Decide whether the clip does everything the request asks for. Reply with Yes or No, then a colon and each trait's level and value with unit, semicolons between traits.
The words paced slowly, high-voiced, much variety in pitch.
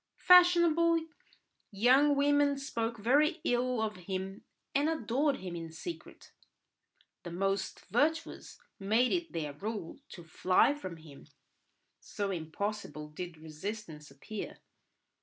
Yes: slow, 115 wpm; high, 215 Hz; wide, 8.5 semitones